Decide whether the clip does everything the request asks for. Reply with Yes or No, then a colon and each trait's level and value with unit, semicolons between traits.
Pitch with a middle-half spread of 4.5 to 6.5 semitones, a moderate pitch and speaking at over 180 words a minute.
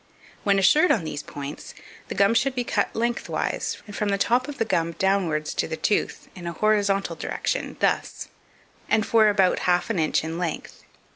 No: average, 4.8 semitones; high, 200 Hz; average, 190 wpm